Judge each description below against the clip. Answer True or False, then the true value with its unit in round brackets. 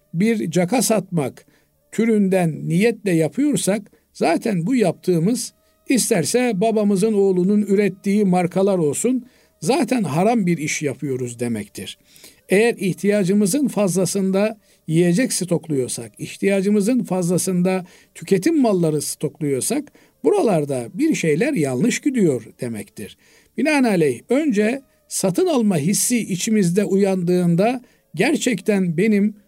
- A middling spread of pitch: True (4.4 semitones)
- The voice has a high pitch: True (195 Hz)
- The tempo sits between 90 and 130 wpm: True (95 wpm)